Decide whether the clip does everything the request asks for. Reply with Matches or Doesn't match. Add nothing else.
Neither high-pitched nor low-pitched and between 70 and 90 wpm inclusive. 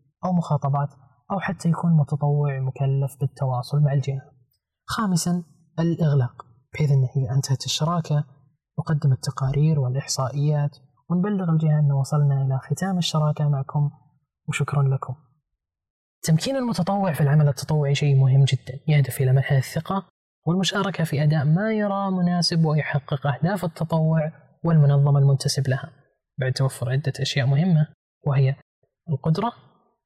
Doesn't match